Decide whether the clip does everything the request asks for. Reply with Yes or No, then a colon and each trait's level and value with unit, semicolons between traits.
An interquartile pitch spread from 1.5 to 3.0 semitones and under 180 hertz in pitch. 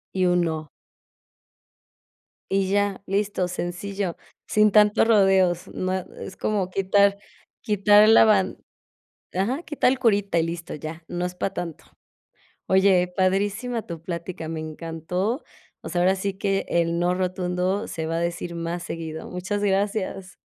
No: average, 2.7 semitones; medium, 185 Hz